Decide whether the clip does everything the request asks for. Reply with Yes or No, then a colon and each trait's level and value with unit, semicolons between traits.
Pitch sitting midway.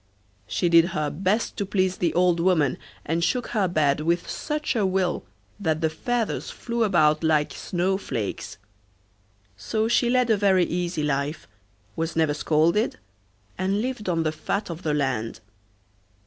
Yes: medium, 175 Hz